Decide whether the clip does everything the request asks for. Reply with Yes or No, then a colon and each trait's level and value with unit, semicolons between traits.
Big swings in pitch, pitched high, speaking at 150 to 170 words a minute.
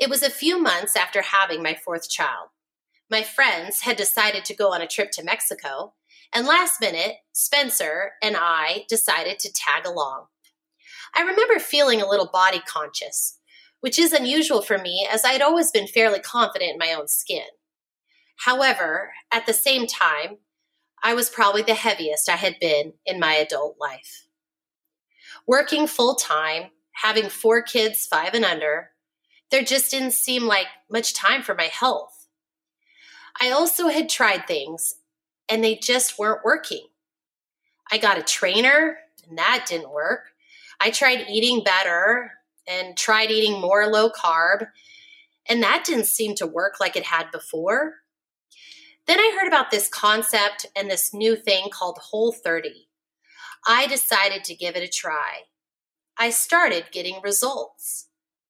Yes: wide, 7.3 semitones; high, 225 Hz; average, 155 wpm